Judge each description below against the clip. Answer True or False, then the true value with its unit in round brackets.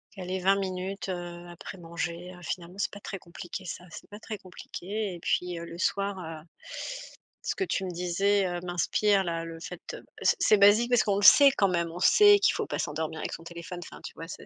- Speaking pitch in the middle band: True (180 Hz)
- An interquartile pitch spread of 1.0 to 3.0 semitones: True (2.7 semitones)